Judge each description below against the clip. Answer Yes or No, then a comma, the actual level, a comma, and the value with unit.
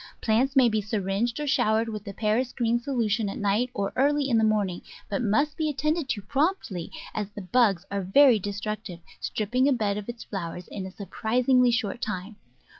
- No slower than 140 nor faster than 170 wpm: No, average, 195 wpm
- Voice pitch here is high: Yes, high, 220 Hz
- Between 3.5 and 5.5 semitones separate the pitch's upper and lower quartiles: Yes, average, 3.8 semitones